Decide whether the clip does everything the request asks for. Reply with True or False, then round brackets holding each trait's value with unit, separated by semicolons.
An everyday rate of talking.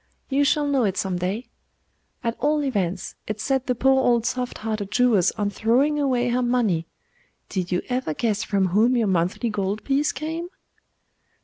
True (175 wpm)